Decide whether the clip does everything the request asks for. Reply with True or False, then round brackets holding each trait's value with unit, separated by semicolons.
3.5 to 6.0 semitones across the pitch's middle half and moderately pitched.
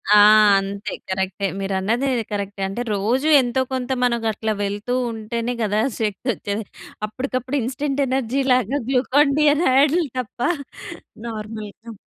False (4.1 semitones; 230 Hz)